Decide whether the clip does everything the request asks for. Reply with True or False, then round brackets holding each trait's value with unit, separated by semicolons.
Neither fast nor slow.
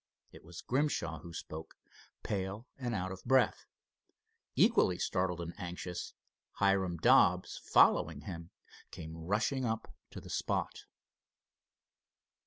False (115 wpm)